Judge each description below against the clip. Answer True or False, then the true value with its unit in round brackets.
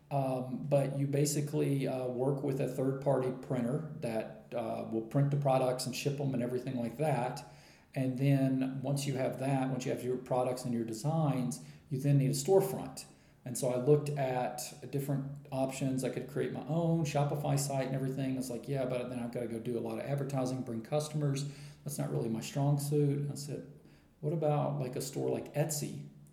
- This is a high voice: False (135 Hz)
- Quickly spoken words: True (210 wpm)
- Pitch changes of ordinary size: False (2.2 semitones)